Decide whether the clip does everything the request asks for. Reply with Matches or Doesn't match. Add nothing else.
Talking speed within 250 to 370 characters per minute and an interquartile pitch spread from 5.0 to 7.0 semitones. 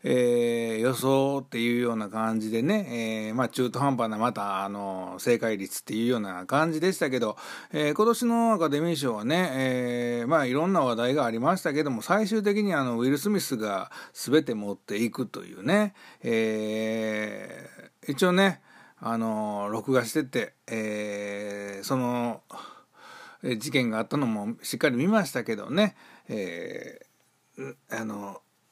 Matches